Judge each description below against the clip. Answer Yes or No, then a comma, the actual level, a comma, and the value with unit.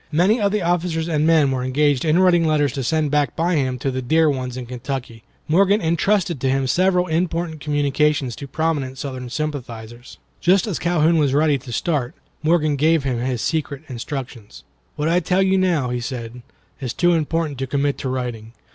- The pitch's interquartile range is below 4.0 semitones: No, average, 4.3 semitones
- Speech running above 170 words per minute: Yes, average, 190 wpm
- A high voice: No, medium, 150 Hz